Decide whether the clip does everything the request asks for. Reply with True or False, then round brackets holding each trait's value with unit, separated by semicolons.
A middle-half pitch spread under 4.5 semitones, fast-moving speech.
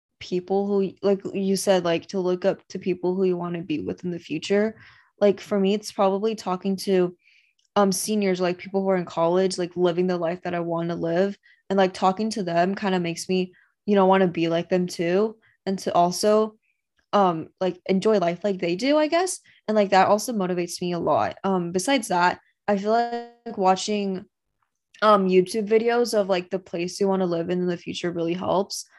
True (2.5 semitones; 215 wpm)